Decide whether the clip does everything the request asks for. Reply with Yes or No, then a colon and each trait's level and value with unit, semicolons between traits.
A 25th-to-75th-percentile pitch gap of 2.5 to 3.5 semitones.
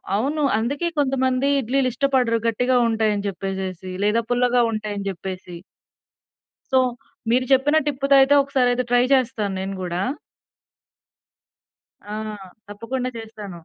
No: average, 4.3 semitones